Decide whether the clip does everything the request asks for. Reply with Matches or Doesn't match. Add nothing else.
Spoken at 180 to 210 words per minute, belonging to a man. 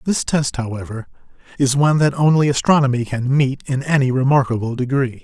Doesn't match